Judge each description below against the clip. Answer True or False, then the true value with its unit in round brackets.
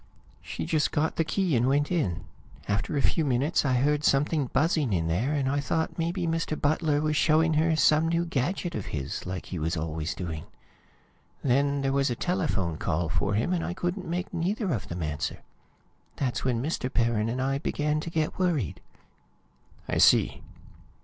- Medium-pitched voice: True (145 Hz)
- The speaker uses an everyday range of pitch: False (6.1 semitones)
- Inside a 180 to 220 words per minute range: True (185 wpm)